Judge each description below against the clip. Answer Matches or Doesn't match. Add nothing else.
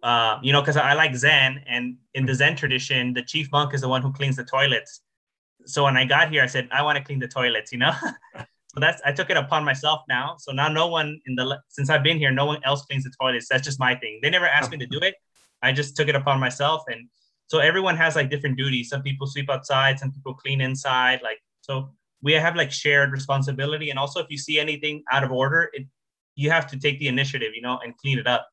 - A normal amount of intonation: Doesn't match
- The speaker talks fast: Matches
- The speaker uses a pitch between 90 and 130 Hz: Doesn't match